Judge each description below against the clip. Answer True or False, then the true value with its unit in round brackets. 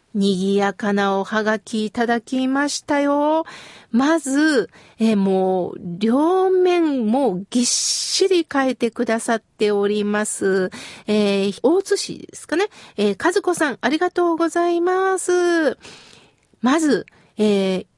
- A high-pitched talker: True (240 Hz)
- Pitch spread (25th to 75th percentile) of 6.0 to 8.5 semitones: True (7.8 semitones)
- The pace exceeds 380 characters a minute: False (235 characters per minute)